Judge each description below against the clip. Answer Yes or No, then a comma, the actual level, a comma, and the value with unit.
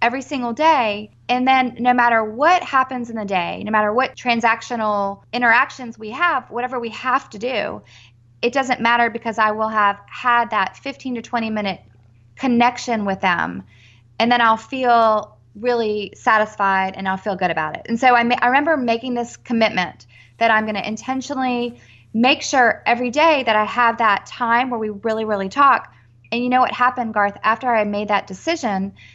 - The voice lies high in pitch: Yes, high, 230 Hz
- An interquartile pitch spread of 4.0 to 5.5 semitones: No, average, 3.5 semitones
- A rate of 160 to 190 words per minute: Yes, average, 185 wpm